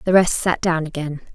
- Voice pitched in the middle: Yes, medium, 165 Hz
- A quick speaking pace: Yes, fast, 225 wpm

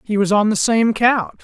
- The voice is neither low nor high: No, high, 215 Hz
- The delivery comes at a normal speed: No, fast, 250 wpm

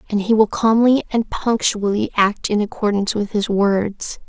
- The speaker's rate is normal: Yes, average, 170 wpm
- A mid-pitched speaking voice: No, high, 210 Hz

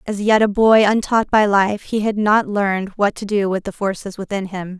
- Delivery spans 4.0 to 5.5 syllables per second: Yes, 5.0 syllables/s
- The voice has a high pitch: Yes, high, 205 Hz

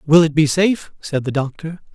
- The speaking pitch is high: No, medium, 155 Hz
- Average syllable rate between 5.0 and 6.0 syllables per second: Yes, 5.5 syllables/s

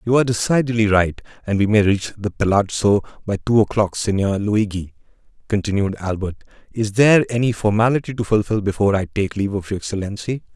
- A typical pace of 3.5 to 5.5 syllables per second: No, 6.1 syllables/s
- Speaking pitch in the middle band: No, low, 105 Hz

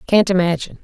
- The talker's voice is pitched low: No, medium, 185 Hz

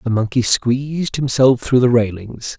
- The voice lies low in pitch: Yes, low, 125 Hz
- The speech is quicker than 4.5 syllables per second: No, 4.4 syllables/s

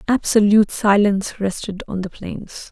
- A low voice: No, high, 205 Hz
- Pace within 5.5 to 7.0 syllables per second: No, 4.8 syllables/s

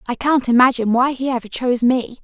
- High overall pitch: Yes, very high, 250 Hz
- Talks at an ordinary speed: No, fast, 215 wpm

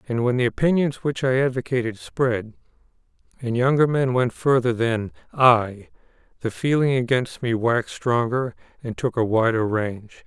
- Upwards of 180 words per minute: No, average, 150 wpm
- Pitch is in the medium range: No, low, 125 Hz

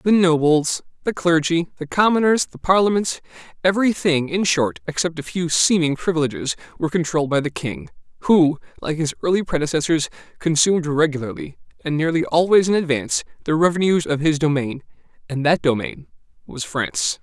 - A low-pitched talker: No, medium, 160 Hz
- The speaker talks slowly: No, average, 150 wpm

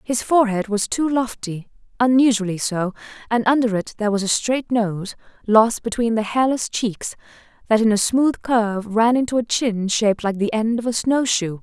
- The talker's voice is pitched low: No, high, 225 Hz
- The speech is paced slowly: No, average, 180 wpm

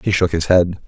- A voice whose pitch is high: No, very low, 90 Hz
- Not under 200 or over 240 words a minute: No, fast, 275 wpm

